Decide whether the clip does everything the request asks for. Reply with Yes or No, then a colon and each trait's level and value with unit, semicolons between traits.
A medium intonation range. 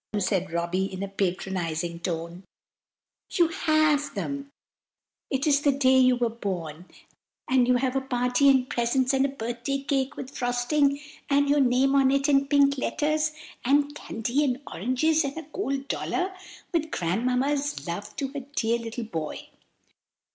Yes: average, 4.1 semitones